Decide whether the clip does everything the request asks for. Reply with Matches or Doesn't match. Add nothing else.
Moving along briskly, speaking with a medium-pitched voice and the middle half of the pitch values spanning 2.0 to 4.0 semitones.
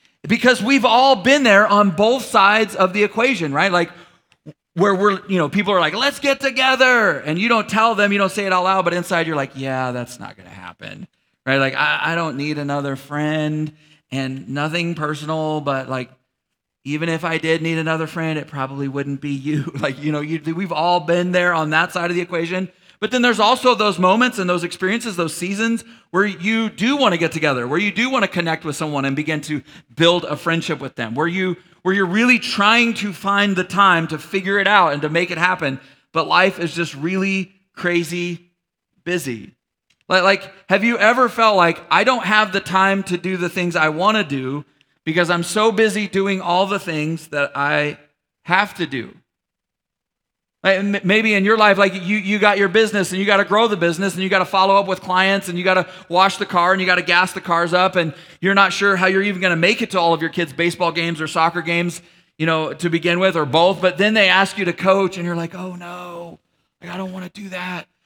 Matches